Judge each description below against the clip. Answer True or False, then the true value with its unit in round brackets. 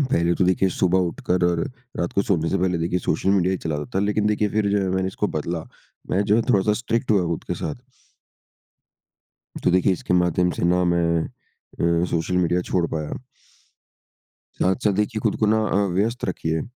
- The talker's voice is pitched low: True (90 Hz)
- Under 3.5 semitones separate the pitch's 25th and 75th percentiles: True (2.8 semitones)